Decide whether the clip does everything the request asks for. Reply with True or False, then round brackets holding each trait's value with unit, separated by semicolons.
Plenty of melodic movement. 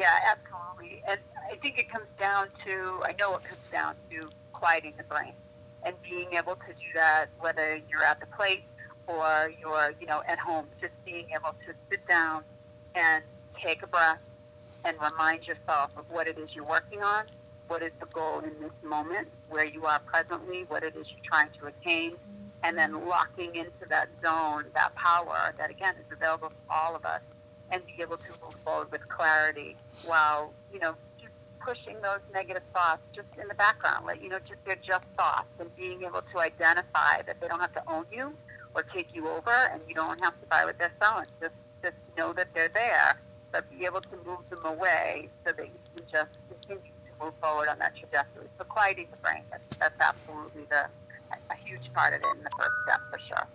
False (3.4 semitones)